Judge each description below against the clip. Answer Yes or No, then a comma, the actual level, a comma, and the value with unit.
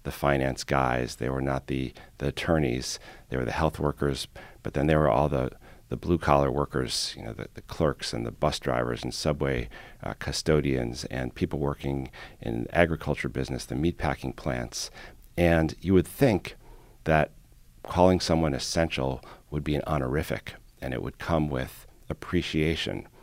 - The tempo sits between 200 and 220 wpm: No, average, 165 wpm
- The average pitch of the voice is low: Yes, very low, 70 Hz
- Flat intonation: No, average, 3.1 semitones